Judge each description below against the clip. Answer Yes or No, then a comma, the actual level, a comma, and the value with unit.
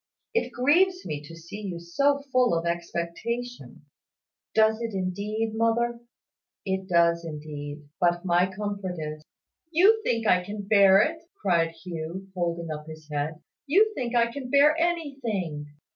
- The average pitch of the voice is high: Yes, high, 195 Hz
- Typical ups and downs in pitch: No, wide, 6.4 semitones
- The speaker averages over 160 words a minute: No, average, 155 wpm